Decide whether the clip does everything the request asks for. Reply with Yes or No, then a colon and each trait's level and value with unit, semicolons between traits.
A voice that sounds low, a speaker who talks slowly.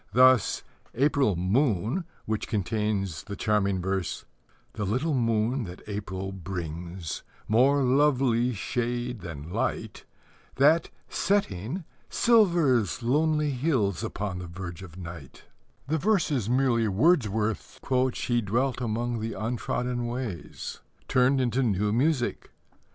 Yes: low, 115 Hz; slow, 110 wpm